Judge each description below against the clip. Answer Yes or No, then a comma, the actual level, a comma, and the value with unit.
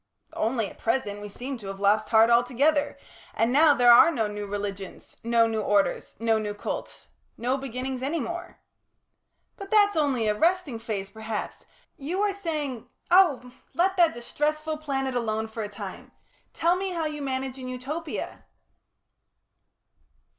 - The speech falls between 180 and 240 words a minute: No, average, 160 wpm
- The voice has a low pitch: No, very high, 255 Hz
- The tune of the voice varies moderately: No, wide, 5.7 semitones